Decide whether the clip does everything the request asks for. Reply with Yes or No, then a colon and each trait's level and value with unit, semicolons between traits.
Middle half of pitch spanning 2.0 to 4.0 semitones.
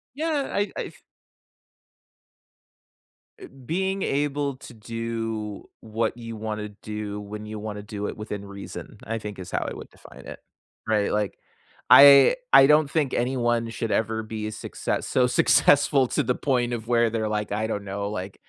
Yes: average, 3.5 semitones